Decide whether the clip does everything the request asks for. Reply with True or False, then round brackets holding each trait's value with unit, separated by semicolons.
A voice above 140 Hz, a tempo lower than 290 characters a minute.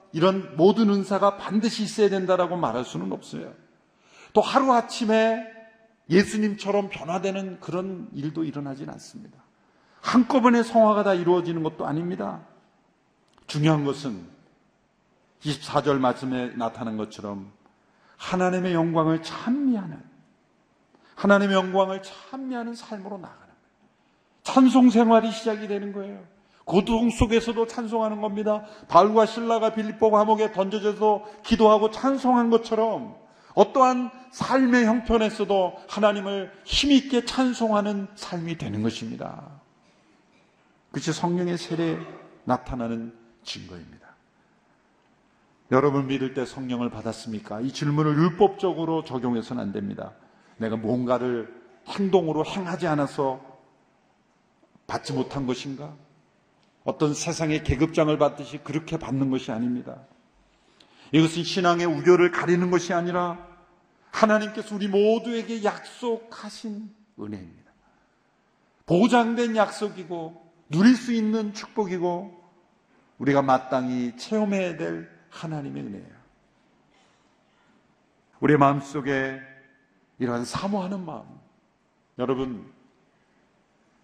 True (185 Hz; 270 characters per minute)